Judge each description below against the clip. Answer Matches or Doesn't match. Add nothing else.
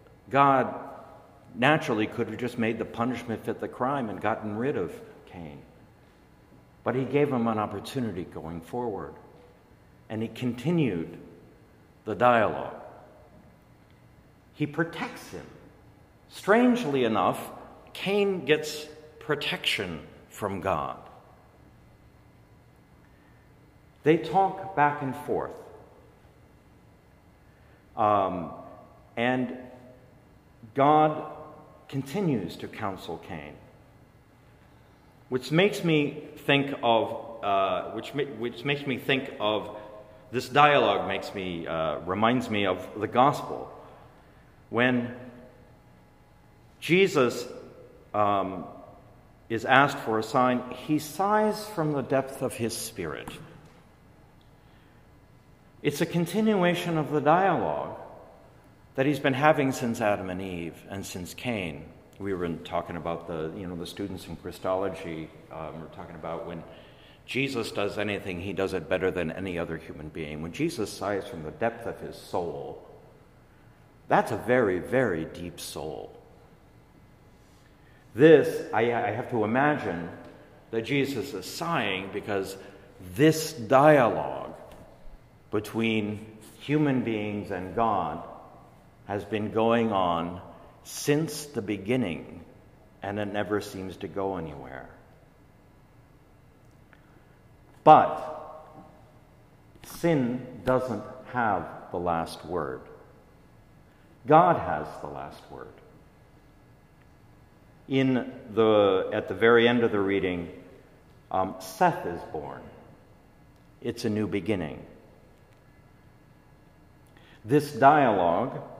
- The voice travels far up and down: Matches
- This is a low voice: Matches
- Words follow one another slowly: Matches